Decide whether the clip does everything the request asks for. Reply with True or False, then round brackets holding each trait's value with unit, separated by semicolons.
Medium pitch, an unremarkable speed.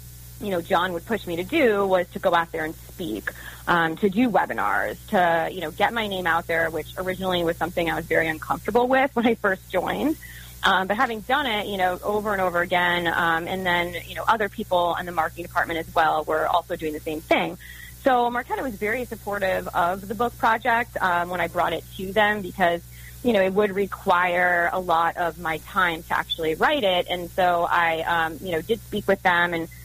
False (175 Hz; 225 wpm)